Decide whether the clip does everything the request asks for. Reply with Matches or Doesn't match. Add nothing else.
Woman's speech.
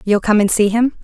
Matches